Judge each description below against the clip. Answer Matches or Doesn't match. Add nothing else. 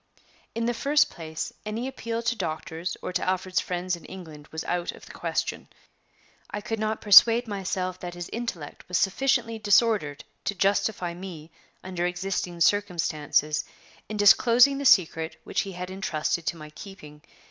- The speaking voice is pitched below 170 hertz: Doesn't match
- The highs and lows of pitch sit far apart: Doesn't match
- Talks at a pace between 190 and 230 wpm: Doesn't match